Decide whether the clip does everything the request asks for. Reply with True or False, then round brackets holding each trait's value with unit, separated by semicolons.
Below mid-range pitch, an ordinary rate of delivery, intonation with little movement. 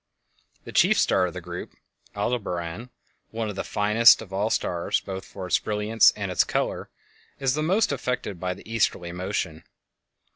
False (100 Hz; 170 wpm; 3.9 semitones)